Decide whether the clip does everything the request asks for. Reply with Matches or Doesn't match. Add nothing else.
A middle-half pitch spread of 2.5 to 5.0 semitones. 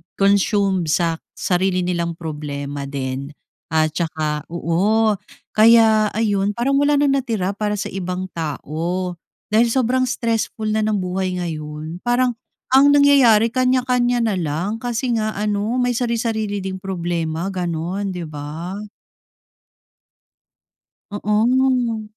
Doesn't match